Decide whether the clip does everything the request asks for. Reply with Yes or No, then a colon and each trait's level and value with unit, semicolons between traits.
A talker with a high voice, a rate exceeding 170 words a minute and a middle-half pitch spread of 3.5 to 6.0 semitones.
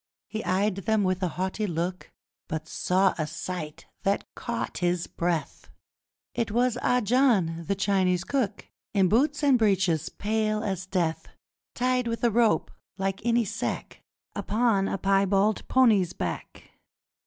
No: high, 195 Hz; average, 140 wpm; average, 3.8 semitones